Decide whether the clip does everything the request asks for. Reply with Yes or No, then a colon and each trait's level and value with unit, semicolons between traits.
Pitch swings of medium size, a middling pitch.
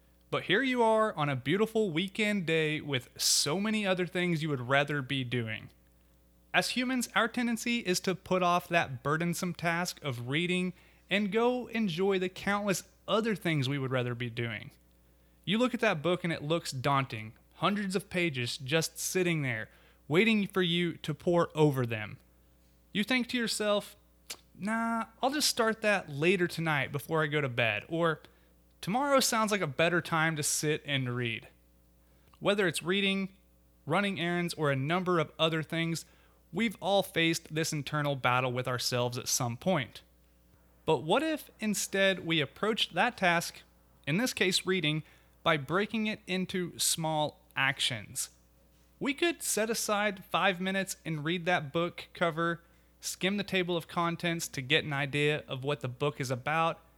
No: wide, 6.1 semitones; medium, 165 Hz